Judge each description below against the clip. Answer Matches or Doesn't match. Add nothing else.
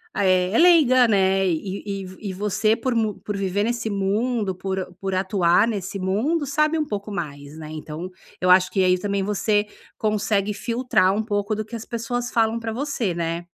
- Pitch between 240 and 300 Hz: Doesn't match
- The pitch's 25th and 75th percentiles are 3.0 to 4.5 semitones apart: Matches